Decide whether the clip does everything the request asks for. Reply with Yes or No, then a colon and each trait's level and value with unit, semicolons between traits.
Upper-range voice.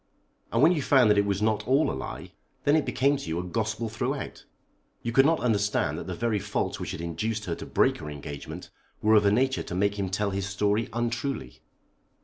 No: low, 110 Hz